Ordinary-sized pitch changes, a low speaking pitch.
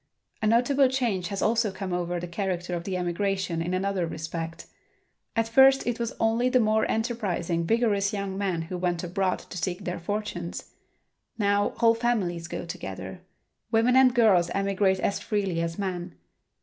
No: average, 4.2 semitones; high, 195 Hz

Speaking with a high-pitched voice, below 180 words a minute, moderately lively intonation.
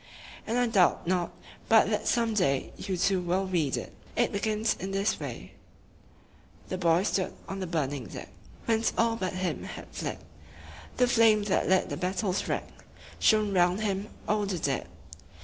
Yes: high, 195 Hz; average, 165 wpm; average, 3.1 semitones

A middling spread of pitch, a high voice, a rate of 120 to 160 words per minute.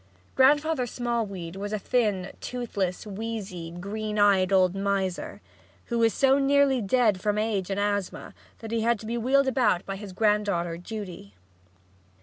Yes: average, 3.6 semitones; high, 210 Hz; average, 150 wpm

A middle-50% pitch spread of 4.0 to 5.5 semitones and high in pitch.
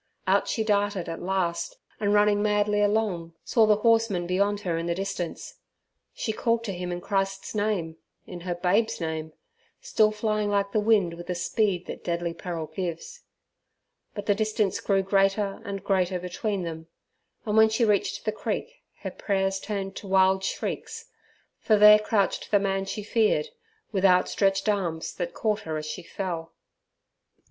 No: average, 3.0 semitones; high, 195 Hz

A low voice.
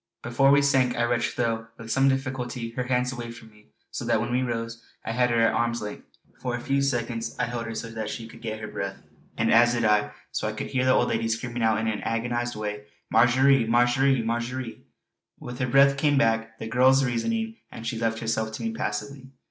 Yes: low, 120 Hz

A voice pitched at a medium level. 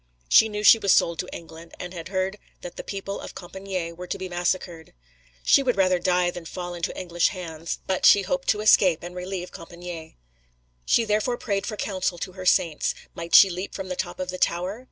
Yes: medium, 180 Hz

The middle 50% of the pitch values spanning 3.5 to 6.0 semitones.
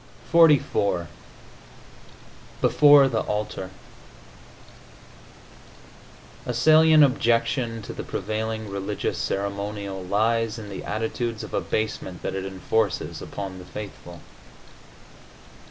No: average, 3.1 semitones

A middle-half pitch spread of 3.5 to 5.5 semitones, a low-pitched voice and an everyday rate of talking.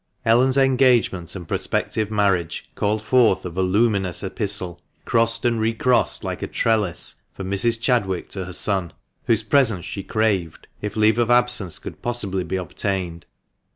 Yes: average, 3.8 semitones; low, 105 Hz; average, 150 wpm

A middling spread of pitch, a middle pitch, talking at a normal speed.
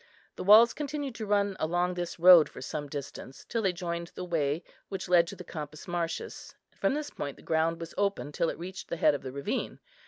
No: average, 3.8 semitones; medium, 175 Hz; fast, 225 wpm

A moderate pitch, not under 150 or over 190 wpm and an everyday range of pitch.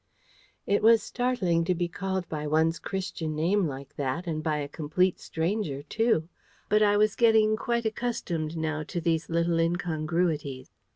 Yes: medium, 170 Hz; average, 160 wpm; average, 4.7 semitones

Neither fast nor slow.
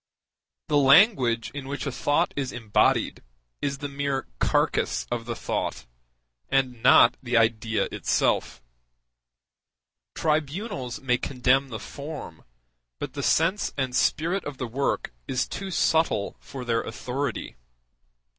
No: slow, 125 wpm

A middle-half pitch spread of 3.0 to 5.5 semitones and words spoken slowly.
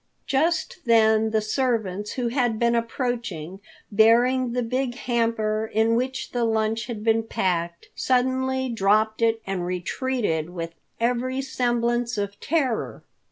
No: narrow, 2.6 semitones; slow, 130 wpm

